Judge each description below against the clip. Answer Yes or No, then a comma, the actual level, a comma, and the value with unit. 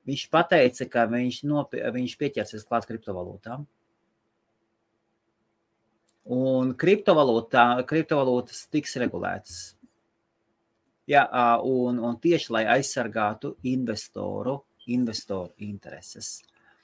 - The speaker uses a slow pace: Yes, slow, 70 wpm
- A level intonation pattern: No, average, 3.7 semitones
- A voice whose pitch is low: Yes, low, 125 Hz